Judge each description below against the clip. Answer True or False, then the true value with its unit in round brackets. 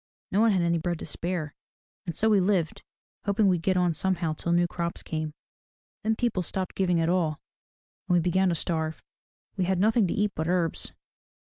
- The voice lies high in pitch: False (180 Hz)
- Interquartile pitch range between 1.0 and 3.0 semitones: True (2.5 semitones)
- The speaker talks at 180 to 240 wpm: True (200 wpm)